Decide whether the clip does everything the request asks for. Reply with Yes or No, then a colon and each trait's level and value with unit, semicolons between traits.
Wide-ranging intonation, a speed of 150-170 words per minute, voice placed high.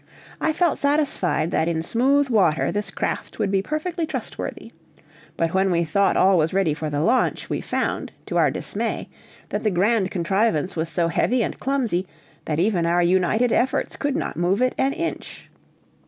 No: wide, 6.9 semitones; average, 180 wpm; high, 195 Hz